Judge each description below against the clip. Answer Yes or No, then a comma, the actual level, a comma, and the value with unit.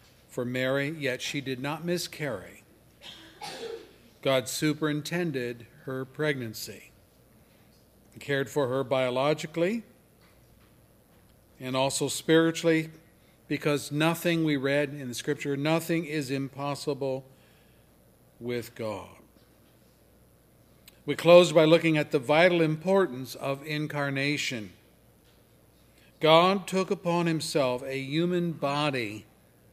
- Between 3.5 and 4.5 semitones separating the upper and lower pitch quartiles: Yes, average, 3.8 semitones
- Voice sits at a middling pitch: Yes, medium, 145 Hz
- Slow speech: Yes, slow, 95 wpm